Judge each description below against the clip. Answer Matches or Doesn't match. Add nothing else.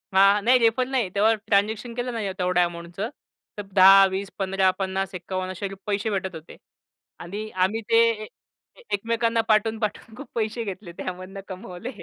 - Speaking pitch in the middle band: Doesn't match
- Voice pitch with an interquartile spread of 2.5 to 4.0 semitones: Matches